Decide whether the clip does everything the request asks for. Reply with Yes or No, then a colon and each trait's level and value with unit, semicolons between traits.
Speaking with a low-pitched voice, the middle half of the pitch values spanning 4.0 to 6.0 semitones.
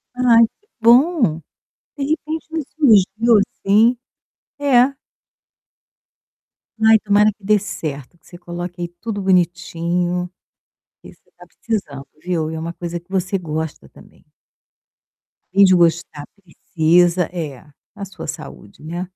No: medium, 185 Hz; average, 4.6 semitones